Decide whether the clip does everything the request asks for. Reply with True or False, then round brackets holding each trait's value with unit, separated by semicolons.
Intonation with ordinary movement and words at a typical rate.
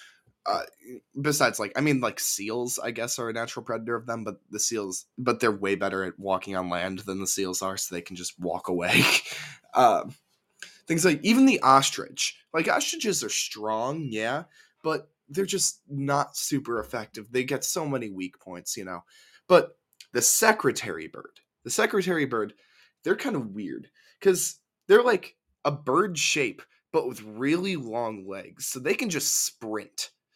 False (7.4 semitones; 175 wpm)